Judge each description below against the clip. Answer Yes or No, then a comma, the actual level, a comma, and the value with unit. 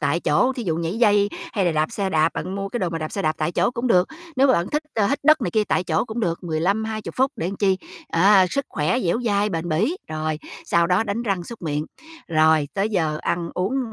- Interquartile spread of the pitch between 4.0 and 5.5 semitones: Yes, average, 5.2 semitones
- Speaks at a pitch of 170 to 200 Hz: Yes, high, 190 Hz